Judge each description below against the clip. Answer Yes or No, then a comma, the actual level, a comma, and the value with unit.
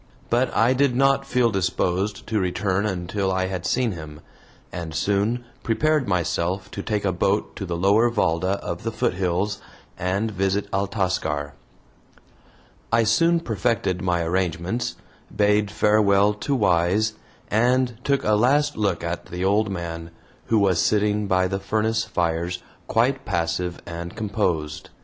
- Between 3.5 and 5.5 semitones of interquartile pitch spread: Yes, average, 3.8 semitones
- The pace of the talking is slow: No, average, 145 wpm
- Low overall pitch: Yes, low, 100 Hz